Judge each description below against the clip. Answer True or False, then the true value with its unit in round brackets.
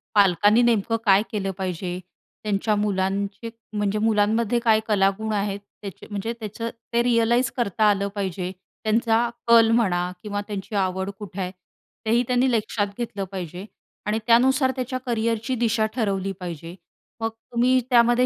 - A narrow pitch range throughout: False (3.0 semitones)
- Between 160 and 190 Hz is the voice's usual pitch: False (215 Hz)